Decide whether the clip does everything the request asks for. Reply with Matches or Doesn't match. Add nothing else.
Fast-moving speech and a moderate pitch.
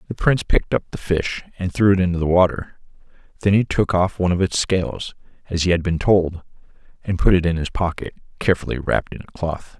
Doesn't match